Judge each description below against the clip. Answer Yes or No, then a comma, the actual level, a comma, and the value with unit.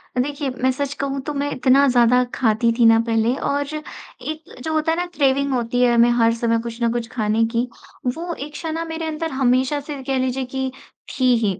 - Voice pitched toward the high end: Yes, very high, 260 Hz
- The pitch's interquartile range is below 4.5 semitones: Yes, average, 3.3 semitones